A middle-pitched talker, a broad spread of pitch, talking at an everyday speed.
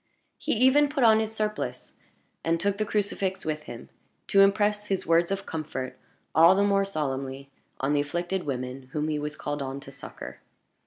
Yes: medium, 170 Hz; wide, 5.9 semitones; average, 180 wpm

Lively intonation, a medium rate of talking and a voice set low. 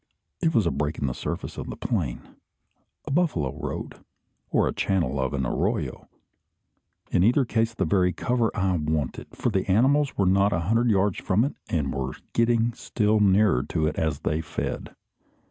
Yes: wide, 6.6 semitones; average, 180 wpm; very low, 95 Hz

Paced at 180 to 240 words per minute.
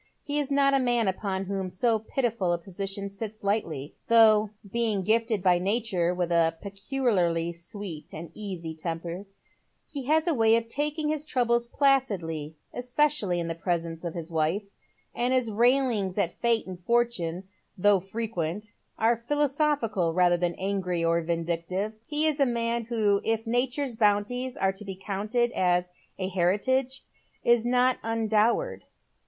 No: average, 160 wpm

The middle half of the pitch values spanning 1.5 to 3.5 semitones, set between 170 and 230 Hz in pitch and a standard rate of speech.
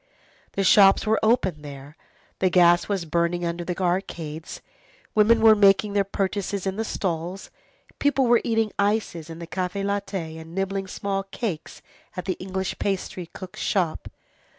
Yes: average, 2.8 semitones; high, 190 Hz; average, 155 wpm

